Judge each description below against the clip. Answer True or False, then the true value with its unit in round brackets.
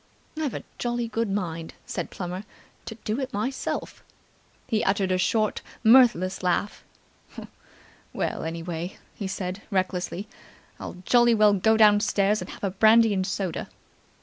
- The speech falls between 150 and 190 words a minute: False (140 wpm)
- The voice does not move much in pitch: False (3.3 semitones)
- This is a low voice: False (205 Hz)